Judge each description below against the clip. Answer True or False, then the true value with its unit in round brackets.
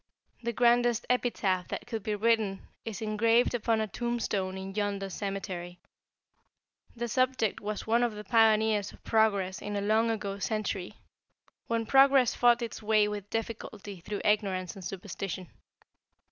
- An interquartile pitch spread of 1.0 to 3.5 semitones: True (2.7 semitones)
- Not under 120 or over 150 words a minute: True (145 wpm)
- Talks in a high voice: True (215 Hz)